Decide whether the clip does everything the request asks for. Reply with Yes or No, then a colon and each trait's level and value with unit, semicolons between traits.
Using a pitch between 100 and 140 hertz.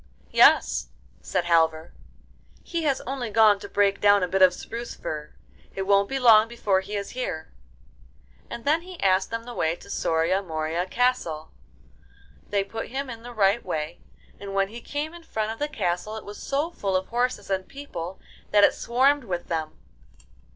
No: high, 205 Hz